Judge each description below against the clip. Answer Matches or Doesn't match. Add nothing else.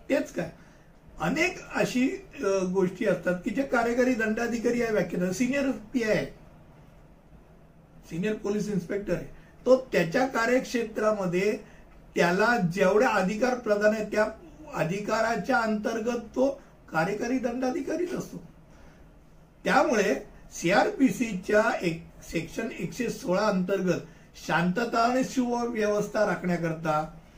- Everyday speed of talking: Doesn't match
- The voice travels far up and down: Doesn't match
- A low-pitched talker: Doesn't match